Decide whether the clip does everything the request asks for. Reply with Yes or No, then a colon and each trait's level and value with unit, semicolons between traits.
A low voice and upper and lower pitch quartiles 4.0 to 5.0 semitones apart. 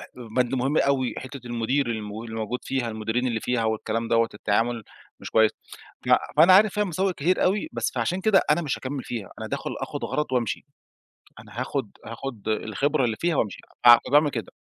Yes: low, 125 Hz; average, 4.3 semitones